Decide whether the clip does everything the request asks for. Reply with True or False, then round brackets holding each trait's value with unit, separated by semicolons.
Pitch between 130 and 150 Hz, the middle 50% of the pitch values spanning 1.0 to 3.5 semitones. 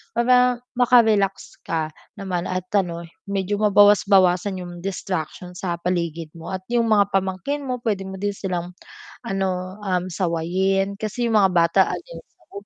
False (195 Hz; 2.6 semitones)